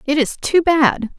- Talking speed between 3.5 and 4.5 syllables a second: Yes, 4.0 syllables/s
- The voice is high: Yes, very high, 290 Hz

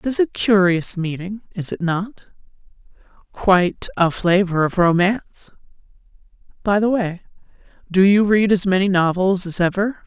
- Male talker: No, female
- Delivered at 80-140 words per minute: Yes, slow, 135 wpm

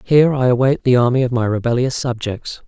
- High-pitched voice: No, low, 125 Hz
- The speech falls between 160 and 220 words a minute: Yes, average, 200 wpm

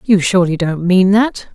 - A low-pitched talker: No, high, 190 Hz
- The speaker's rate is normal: Yes, average, 195 wpm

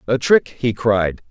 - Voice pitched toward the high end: No, low, 115 Hz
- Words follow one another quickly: No, average, 185 wpm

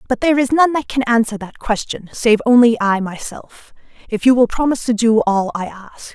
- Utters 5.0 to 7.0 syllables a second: Yes, 5.3 syllables/s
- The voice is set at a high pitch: Yes, high, 235 Hz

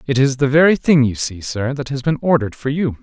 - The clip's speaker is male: Yes, male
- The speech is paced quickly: Yes, fast, 280 wpm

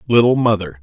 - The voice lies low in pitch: Yes, low, 105 Hz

